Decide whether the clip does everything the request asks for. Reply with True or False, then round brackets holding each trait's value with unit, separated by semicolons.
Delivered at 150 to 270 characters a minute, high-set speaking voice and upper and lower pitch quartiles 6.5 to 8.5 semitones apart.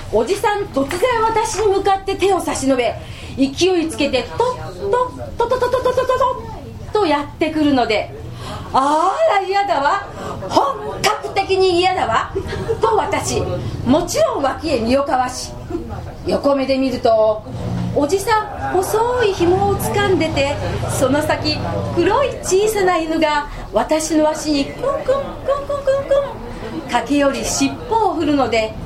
True (255 characters per minute; 345 Hz; 7.1 semitones)